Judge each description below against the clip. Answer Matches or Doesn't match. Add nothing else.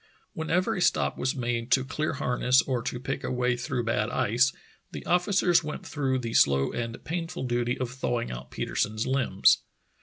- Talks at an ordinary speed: Matches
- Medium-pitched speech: Doesn't match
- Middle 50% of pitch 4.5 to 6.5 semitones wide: Doesn't match